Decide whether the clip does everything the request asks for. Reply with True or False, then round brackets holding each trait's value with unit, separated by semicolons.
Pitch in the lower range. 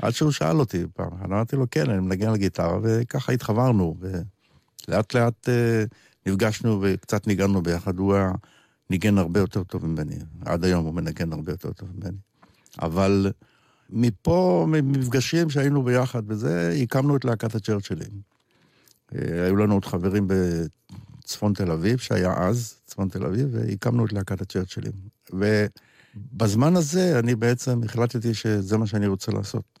True (105 Hz)